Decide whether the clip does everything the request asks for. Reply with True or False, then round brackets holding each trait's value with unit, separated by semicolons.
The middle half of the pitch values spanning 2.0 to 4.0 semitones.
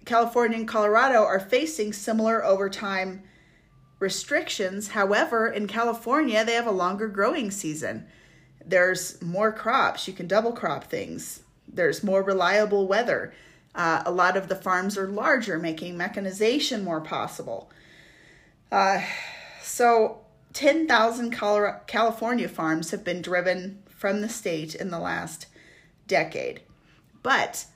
True (3.6 semitones)